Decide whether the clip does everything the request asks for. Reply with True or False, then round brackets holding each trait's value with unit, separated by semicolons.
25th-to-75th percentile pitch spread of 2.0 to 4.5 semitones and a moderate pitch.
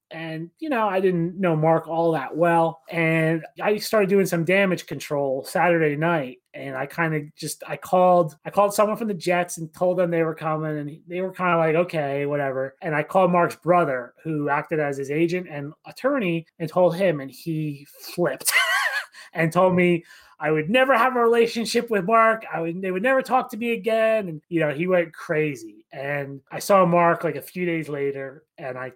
True (3.4 semitones; 165 Hz)